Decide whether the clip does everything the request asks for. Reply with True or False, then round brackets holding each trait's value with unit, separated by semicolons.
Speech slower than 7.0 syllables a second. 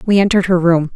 False (7.2 syllables/s)